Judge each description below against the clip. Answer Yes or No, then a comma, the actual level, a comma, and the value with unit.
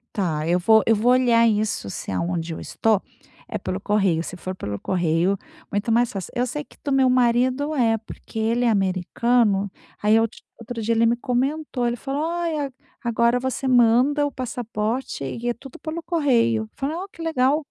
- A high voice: Yes, high, 235 Hz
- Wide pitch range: No, average, 4.1 semitones